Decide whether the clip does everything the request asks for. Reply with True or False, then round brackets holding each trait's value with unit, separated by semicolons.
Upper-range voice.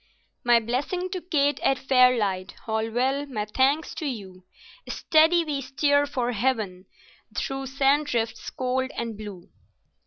True (260 Hz)